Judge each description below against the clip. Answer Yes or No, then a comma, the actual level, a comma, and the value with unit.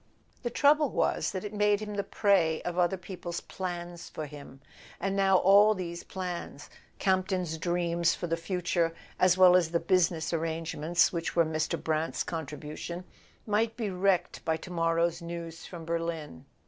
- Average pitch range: No, narrow, 2.3 semitones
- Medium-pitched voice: Yes, medium, 175 Hz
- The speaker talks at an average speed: Yes, average, 155 wpm